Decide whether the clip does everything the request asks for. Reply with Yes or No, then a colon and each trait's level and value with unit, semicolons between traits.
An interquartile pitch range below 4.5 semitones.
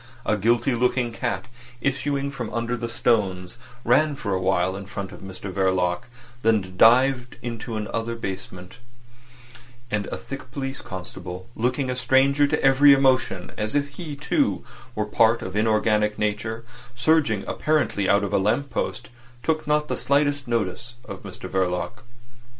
No: average, 5.0 semitones